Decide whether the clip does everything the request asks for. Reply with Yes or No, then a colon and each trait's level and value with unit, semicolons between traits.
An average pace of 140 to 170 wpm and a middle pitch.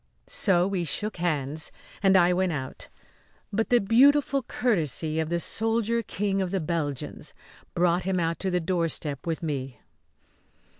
Yes: average, 150 wpm; medium, 175 Hz